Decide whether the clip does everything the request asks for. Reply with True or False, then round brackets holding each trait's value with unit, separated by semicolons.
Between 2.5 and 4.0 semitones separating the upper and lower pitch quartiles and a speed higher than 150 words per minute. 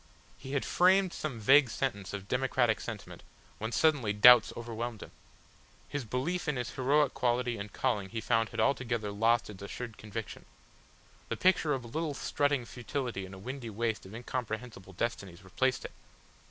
True (3.7 semitones; 165 wpm)